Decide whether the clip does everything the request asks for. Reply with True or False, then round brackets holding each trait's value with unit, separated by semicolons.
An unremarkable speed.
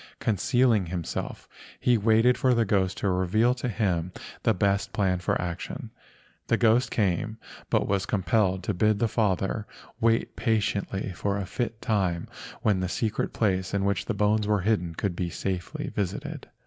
True (170 wpm)